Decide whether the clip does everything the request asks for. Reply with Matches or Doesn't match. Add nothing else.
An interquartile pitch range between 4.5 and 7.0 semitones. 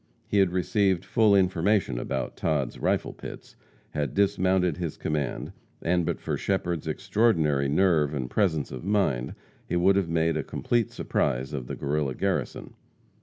Matches